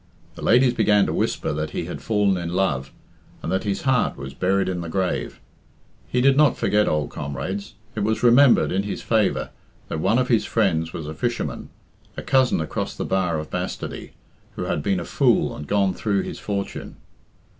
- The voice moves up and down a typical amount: Yes, average, 5.0 semitones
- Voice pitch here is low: Yes, low, 100 Hz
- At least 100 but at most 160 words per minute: No, average, 195 wpm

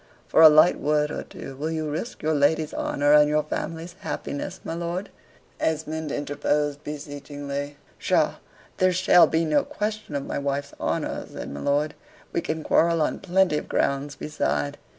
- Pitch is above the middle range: No, medium, 150 Hz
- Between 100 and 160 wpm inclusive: No, average, 170 wpm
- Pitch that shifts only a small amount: Yes, narrow, 2.1 semitones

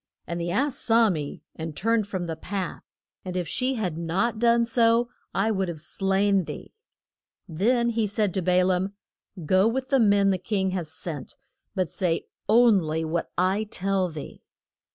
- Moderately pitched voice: No, high, 195 Hz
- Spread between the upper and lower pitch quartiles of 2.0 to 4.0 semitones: No, average, 4.4 semitones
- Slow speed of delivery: No, average, 180 wpm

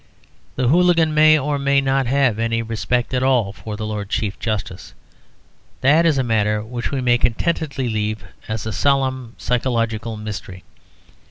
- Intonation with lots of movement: No, average, 4.0 semitones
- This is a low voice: Yes, low, 120 Hz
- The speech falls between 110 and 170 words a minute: Yes, average, 160 wpm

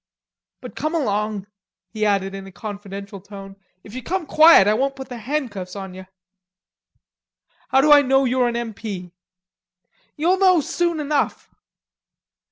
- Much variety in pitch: Yes, wide, 6.4 semitones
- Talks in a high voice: Yes, high, 225 Hz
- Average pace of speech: Yes, average, 155 wpm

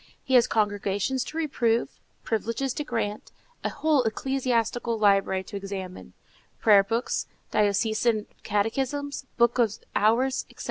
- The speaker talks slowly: Yes, slow, 120 wpm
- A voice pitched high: Yes, high, 230 Hz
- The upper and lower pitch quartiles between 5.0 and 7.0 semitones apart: No, average, 3.9 semitones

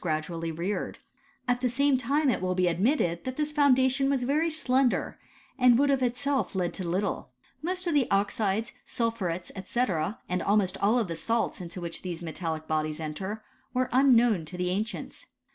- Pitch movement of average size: No, wide, 6.5 semitones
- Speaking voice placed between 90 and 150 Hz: No, high, 220 Hz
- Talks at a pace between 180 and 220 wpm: Yes, average, 185 wpm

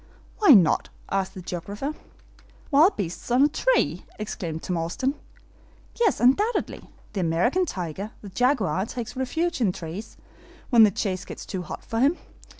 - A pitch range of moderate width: No, wide, 7.2 semitones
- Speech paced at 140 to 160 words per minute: Yes, average, 155 wpm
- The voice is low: No, high, 220 Hz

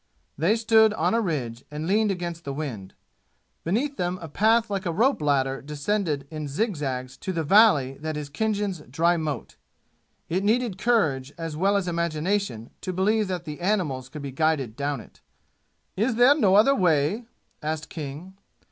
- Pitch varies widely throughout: Yes, wide, 6.1 semitones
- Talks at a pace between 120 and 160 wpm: No, average, 170 wpm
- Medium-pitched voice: Yes, medium, 170 Hz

